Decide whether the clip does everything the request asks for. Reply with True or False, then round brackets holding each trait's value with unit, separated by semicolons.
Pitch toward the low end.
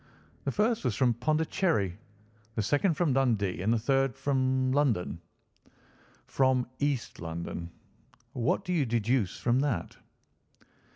True (130 Hz)